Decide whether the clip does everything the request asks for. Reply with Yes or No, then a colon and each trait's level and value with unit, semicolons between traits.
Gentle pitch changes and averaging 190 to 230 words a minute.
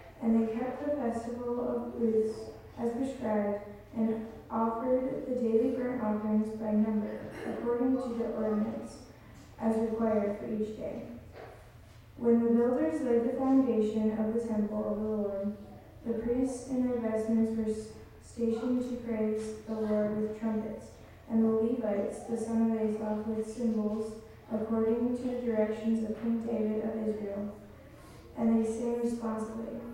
No: narrow, 1.6 semitones; average, 145 wpm